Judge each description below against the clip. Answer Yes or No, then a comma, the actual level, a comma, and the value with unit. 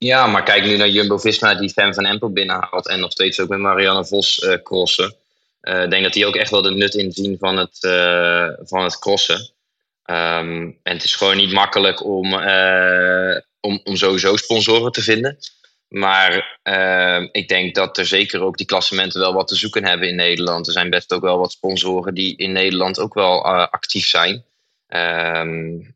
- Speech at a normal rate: Yes, average, 195 wpm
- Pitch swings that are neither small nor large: No, narrow, 1.8 semitones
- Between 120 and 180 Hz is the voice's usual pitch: No, very low, 95 Hz